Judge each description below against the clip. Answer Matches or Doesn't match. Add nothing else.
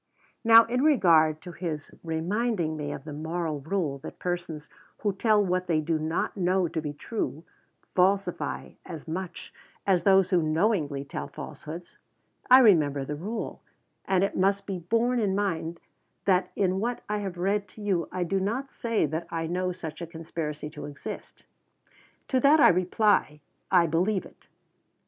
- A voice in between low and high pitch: Matches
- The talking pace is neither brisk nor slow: Matches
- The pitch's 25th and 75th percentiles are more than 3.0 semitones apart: Matches